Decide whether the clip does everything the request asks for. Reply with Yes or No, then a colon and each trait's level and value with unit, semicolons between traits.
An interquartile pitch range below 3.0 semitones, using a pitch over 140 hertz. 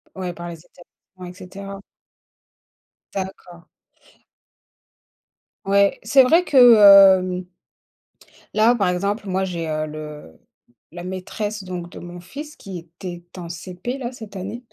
Yes: narrow, 2.4 semitones; medium, 185 Hz